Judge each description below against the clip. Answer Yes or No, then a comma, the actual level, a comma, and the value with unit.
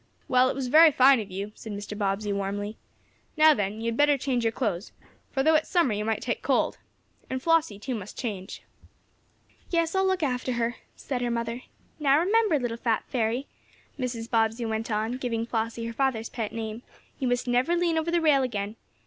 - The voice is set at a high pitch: Yes, high, 240 Hz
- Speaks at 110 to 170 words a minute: No, average, 200 wpm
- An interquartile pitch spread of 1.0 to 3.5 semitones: No, average, 3.9 semitones